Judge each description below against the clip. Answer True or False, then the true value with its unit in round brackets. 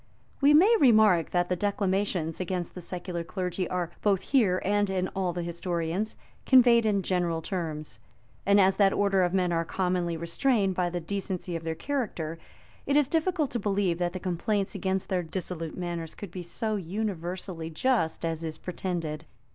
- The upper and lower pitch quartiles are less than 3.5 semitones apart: True (3.0 semitones)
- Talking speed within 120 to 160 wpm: False (175 wpm)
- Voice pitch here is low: False (185 Hz)